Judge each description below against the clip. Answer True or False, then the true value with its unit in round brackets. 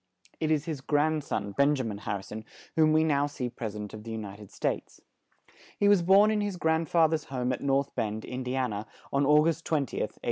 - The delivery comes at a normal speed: False (260 wpm)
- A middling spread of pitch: False (6.0 semitones)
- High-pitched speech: False (140 Hz)